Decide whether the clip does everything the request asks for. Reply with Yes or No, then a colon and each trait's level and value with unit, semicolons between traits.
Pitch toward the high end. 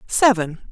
Yes: high, 200 Hz